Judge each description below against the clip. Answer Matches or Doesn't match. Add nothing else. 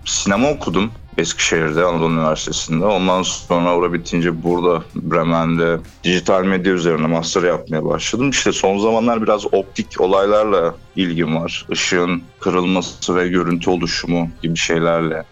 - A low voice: Matches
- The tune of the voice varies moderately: Doesn't match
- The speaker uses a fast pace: Doesn't match